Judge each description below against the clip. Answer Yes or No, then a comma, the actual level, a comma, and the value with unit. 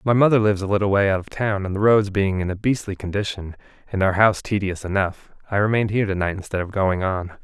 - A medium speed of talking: No, fast, 240 wpm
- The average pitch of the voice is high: No, low, 100 Hz